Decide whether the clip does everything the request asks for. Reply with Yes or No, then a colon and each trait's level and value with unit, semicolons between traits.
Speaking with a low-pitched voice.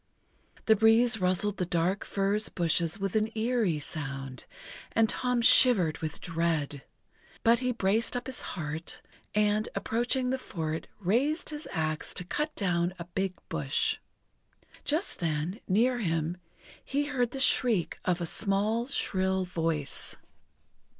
No: high, 195 Hz